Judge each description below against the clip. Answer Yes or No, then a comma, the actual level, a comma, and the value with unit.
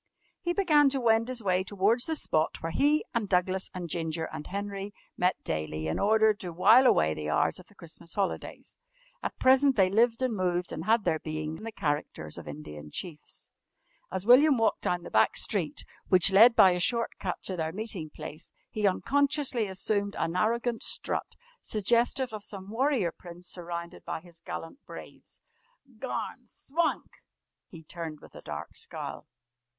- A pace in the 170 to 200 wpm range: Yes, average, 175 wpm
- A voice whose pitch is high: Yes, high, 195 Hz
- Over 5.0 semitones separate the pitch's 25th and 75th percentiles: Yes, wide, 5.6 semitones